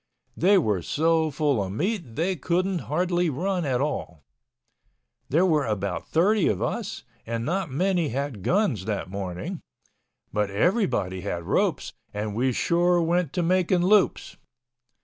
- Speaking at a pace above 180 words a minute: No, average, 140 wpm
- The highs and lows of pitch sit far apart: Yes, wide, 8.8 semitones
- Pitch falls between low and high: Yes, medium, 155 Hz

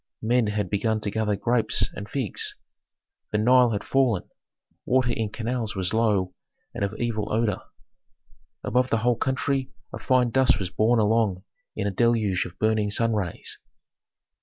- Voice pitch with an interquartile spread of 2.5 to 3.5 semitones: Yes, average, 2.8 semitones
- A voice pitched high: No, low, 110 Hz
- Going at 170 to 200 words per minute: No, average, 160 wpm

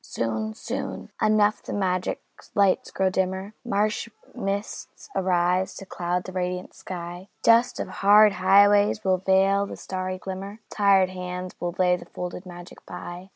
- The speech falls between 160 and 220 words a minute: No, average, 150 wpm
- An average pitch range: No, narrow, 1.7 semitones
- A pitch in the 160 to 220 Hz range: Yes, high, 190 Hz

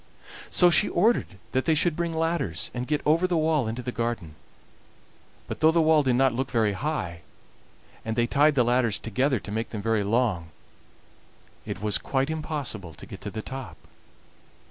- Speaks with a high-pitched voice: No, low, 130 Hz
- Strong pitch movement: Yes, wide, 5.8 semitones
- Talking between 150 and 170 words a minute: No, average, 185 wpm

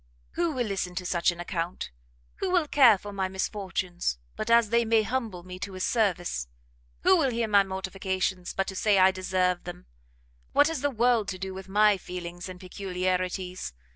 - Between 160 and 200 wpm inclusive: Yes, average, 190 wpm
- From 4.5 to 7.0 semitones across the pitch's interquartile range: No, average, 3.4 semitones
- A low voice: No, high, 190 Hz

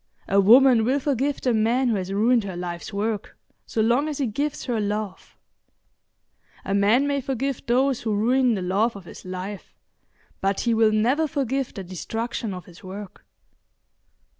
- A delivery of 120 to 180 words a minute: Yes, average, 170 wpm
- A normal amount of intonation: Yes, average, 4.6 semitones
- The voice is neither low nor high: No, high, 225 Hz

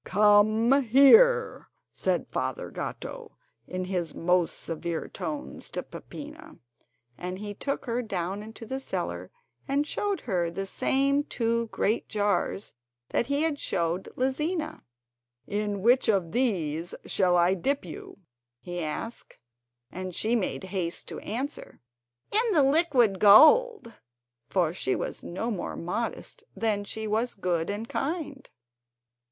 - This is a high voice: Yes, high, 220 Hz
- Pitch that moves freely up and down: Yes, wide, 7.0 semitones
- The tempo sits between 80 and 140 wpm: Yes, slow, 135 wpm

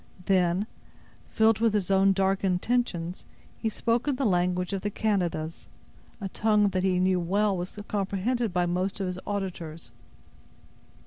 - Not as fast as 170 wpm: Yes, average, 150 wpm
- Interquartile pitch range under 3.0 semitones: Yes, narrow, 2.6 semitones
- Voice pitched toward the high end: Yes, high, 195 Hz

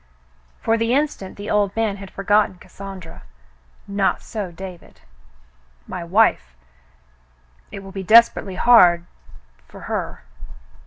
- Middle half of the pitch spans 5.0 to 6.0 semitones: No, average, 2.9 semitones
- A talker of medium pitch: No, high, 195 Hz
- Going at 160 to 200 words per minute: No, slow, 135 wpm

